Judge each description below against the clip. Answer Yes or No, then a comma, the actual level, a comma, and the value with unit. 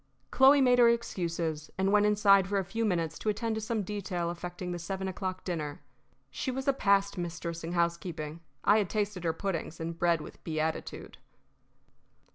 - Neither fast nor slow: Yes, average, 180 wpm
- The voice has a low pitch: No, medium, 185 Hz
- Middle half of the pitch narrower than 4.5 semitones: Yes, average, 3.7 semitones